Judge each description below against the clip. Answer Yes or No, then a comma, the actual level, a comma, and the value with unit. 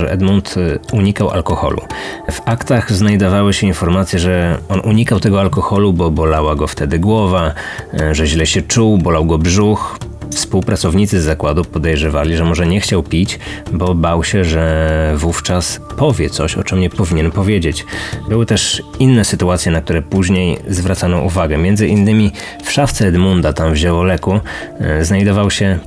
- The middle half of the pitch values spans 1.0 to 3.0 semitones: No, average, 3.6 semitones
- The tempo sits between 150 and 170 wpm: Yes, average, 155 wpm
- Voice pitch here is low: Yes, very low, 95 Hz